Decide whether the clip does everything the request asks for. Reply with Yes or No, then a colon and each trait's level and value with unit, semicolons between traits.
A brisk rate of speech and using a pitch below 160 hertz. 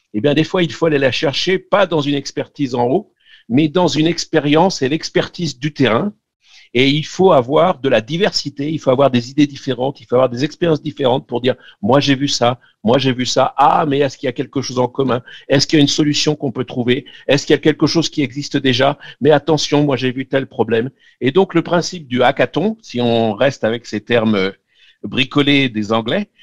Yes: fast, 230 wpm; medium, 140 Hz